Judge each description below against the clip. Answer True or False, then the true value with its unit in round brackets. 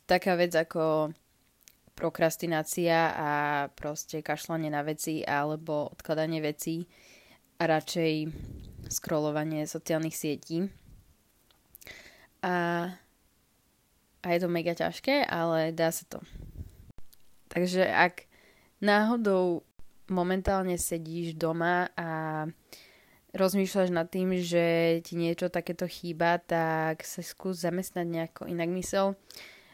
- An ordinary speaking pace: False (100 wpm)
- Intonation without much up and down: True (2.2 semitones)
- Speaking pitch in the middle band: True (165 Hz)